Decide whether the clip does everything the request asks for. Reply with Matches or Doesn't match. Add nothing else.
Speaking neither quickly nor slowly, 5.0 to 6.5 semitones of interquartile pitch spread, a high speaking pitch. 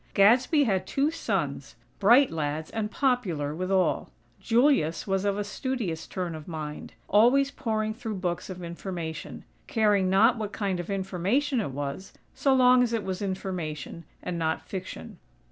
Matches